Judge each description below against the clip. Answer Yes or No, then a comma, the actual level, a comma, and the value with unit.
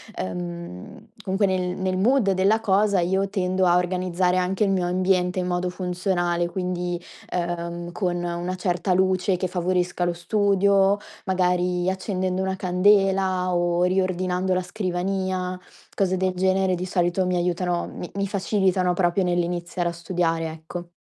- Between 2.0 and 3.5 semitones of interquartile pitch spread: No, narrow, 1.2 semitones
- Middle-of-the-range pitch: Yes, medium, 180 Hz